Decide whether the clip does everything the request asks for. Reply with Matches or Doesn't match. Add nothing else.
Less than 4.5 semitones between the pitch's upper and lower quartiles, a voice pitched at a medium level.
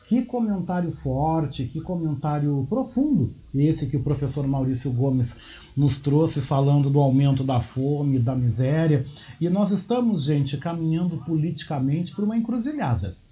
Matches